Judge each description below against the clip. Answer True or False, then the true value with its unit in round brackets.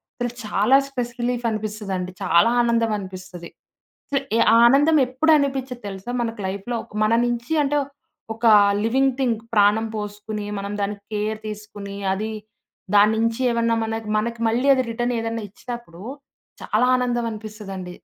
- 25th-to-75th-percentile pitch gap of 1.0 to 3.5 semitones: True (2.8 semitones)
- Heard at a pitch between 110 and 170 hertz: False (225 Hz)